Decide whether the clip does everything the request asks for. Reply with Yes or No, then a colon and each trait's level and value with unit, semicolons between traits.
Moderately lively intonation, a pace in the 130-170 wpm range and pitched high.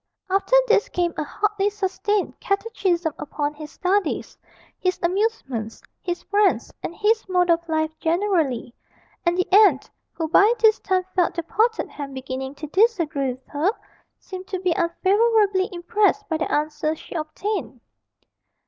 Yes: average, 4.8 semitones; average, 150 wpm; very high, 360 Hz